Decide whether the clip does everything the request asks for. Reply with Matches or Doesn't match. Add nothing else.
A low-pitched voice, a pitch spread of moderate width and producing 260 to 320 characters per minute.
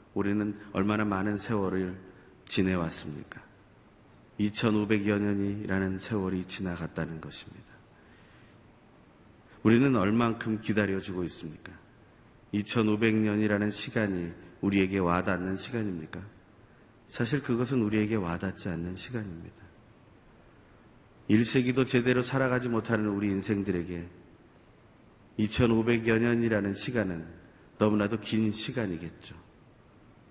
Doesn't match